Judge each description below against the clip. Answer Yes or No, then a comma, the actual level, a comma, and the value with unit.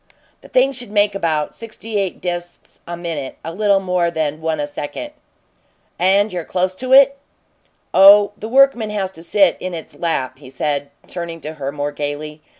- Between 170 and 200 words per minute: Yes, average, 180 wpm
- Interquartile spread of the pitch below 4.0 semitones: No, average, 5.1 semitones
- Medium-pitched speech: Yes, medium, 175 Hz